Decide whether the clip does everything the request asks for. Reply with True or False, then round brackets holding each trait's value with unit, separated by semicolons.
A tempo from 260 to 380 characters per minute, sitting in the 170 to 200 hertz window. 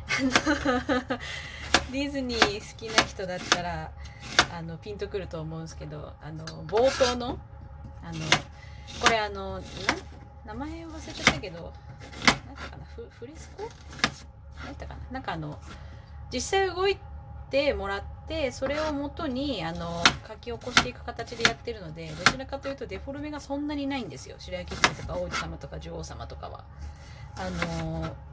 True (300 characters per minute; 185 Hz)